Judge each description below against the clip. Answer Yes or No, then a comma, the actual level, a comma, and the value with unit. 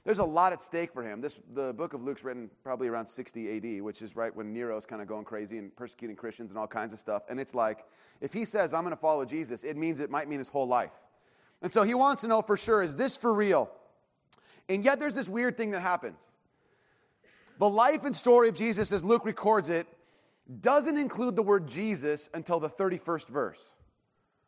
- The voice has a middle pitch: Yes, medium, 170 Hz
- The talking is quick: Yes, fast, 225 wpm